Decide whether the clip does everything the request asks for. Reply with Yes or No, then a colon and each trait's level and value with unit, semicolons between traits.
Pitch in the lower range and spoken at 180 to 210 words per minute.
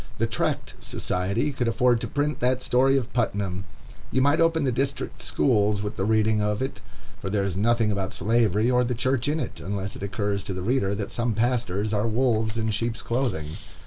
Yes: low, 115 Hz; fast, 205 wpm